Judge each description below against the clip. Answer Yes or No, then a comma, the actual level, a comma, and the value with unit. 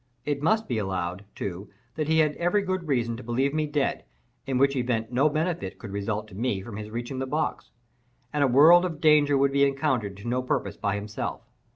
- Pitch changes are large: Yes, wide, 5.8 semitones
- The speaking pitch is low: Yes, low, 130 Hz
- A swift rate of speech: Yes, fast, 215 wpm